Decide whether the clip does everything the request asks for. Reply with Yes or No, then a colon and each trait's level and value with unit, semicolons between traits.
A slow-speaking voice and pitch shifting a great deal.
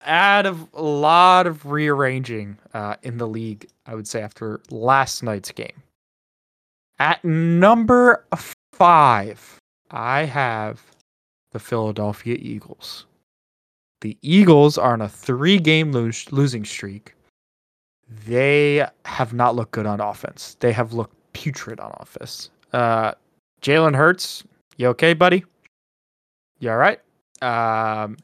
Yes: slow, 125 wpm; wide, 6.2 semitones